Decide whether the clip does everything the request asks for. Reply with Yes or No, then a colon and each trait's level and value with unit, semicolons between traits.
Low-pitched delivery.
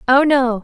No: very high, 260 Hz